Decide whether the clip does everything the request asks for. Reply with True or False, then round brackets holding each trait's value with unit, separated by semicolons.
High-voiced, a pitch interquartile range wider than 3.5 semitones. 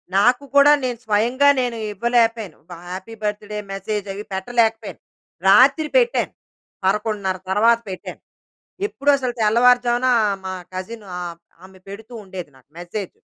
True (215 Hz; 4.1 semitones)